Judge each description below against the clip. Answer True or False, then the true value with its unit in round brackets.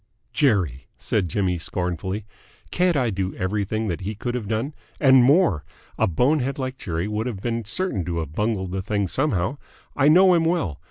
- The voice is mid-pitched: False (110 Hz)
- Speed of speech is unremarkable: True (180 wpm)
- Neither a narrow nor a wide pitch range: False (6.2 semitones)